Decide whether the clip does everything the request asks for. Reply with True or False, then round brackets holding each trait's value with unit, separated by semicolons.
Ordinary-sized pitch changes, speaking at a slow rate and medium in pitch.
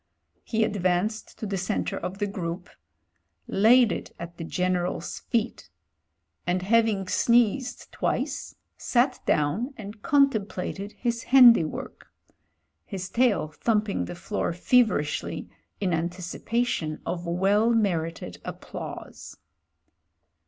False (4.8 semitones; 120 wpm; 195 Hz)